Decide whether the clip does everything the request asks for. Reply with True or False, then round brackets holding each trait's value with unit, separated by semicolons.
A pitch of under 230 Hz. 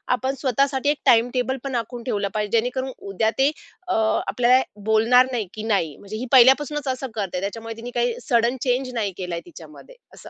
False (240 Hz)